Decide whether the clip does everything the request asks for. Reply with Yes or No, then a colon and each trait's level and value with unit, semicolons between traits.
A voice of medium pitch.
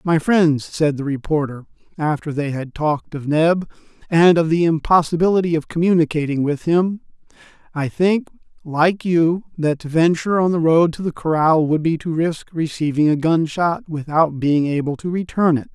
Yes: medium, 160 Hz